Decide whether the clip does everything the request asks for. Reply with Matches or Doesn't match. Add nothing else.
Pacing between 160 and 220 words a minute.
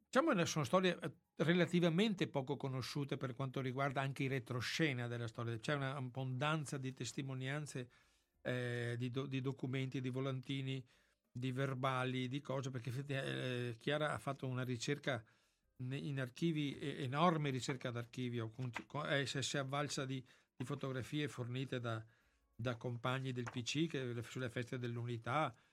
Doesn't match